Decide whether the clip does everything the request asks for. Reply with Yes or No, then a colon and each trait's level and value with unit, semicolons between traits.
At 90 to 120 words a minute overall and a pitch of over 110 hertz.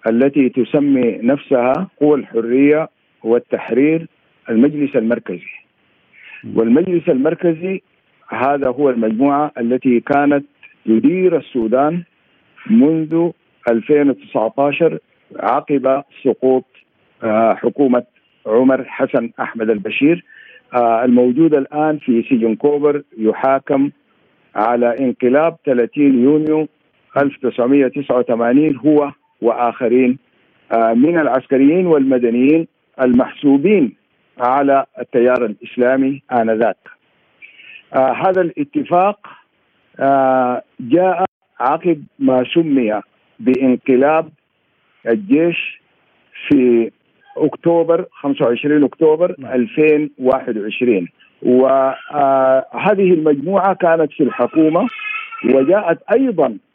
No: average, 75 wpm; medium, 140 Hz